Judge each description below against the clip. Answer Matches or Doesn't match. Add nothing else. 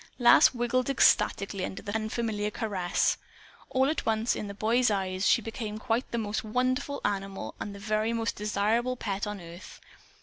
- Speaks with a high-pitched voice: Matches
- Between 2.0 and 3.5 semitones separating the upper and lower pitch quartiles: Matches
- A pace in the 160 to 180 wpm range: Matches